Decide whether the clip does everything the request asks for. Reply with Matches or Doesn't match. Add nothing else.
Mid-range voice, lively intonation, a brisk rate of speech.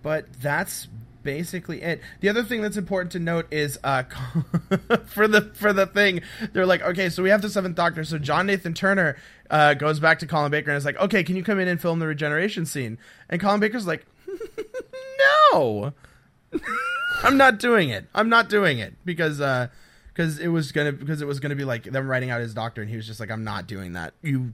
Matches